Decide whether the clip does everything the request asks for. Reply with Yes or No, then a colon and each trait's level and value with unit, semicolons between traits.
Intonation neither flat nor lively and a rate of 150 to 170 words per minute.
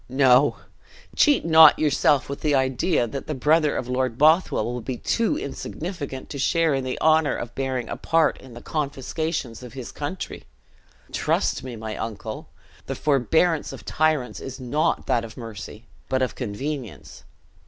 Yes: average, 4.0 semitones; average, 165 wpm